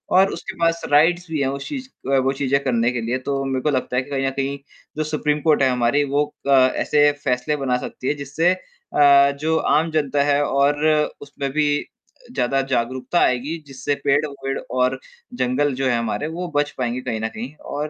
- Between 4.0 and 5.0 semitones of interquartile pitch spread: No, narrow, 2.4 semitones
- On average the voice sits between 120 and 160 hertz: Yes, medium, 140 Hz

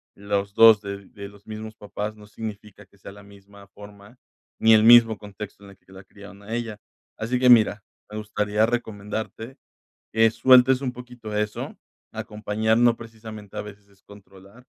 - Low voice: Yes, low, 105 Hz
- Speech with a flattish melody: Yes, narrow, 1.8 semitones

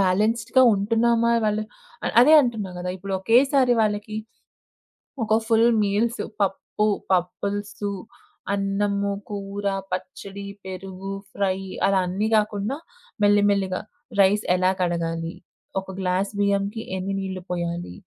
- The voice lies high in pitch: Yes, high, 200 Hz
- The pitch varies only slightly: Yes, narrow, 2.2 semitones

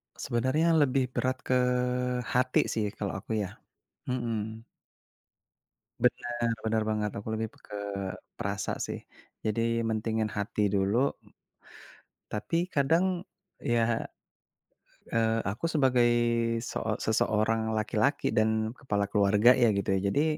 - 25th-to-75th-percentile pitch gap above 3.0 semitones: No, average, 2.7 semitones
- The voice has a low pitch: Yes, low, 110 Hz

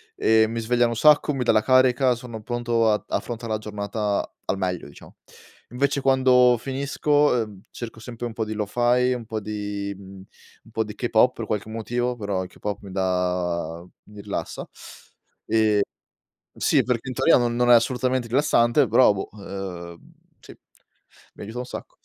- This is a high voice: No, low, 115 Hz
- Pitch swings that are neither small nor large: Yes, average, 3.3 semitones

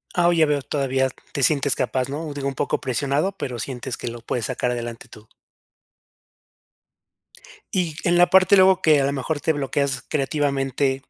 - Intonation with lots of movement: No, average, 3.1 semitones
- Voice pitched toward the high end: No, medium, 140 Hz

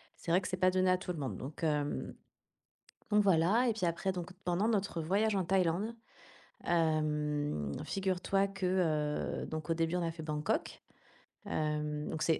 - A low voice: No, medium, 170 Hz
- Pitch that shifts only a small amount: No, average, 3.7 semitones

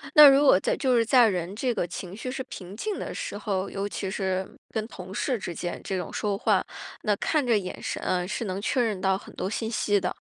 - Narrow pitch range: No, average, 4.1 semitones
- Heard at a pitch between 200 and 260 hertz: Yes, high, 205 Hz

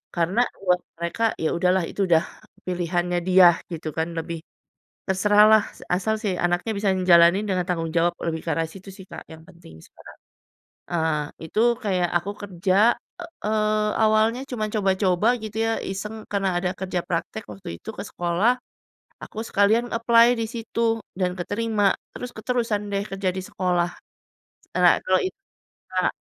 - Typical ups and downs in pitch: Yes, average, 3.5 semitones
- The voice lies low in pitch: No, high, 190 Hz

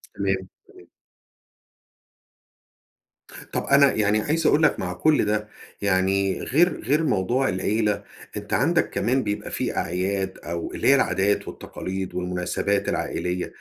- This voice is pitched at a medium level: No, low, 100 Hz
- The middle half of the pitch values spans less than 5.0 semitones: No, wide, 5.5 semitones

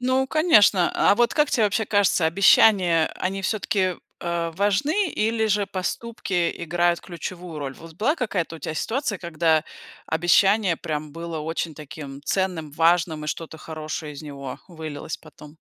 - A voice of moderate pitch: Yes, medium, 175 Hz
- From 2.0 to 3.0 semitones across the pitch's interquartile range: No, average, 4.4 semitones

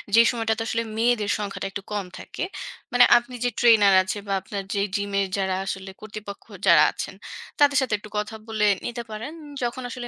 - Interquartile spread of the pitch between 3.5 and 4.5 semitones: No, average, 3.0 semitones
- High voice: Yes, high, 215 Hz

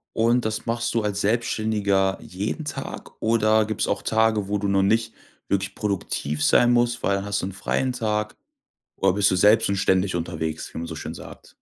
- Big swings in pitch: No, narrow, 2.5 semitones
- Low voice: Yes, low, 105 Hz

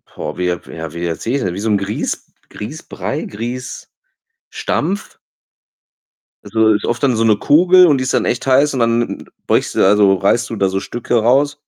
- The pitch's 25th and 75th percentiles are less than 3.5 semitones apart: No, average, 4.8 semitones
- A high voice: No, low, 115 Hz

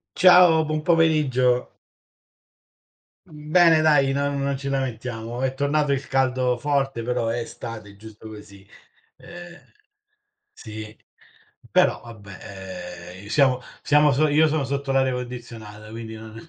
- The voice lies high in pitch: No, low, 130 Hz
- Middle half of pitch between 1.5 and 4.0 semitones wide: No, average, 4.8 semitones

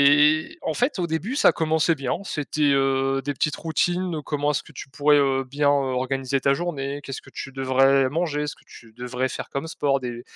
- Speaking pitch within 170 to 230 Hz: No, medium, 140 Hz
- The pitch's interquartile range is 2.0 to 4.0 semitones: Yes, narrow, 2.6 semitones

